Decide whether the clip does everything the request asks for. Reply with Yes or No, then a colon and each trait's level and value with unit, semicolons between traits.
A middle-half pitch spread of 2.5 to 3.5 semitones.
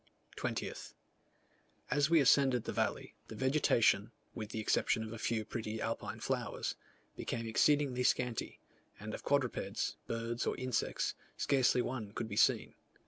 Yes: average, 3.0 semitones